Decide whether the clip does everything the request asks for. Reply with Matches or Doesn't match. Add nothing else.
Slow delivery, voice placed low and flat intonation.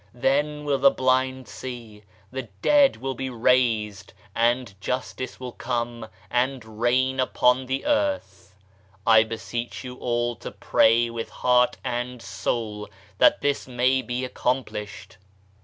Matches